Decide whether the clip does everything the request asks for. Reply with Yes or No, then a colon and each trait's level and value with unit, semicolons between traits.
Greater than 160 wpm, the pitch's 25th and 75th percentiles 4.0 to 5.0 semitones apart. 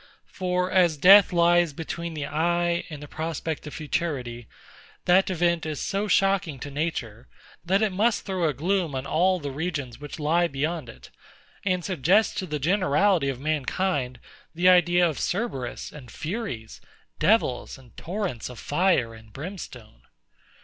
No: average, 155 wpm; average, 4.6 semitones